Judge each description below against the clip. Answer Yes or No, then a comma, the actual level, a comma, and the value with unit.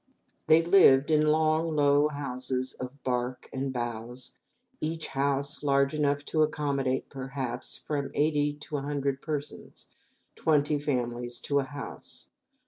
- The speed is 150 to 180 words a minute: No, slow, 135 wpm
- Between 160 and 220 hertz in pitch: No, medium, 140 Hz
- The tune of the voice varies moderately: No, narrow, 2.3 semitones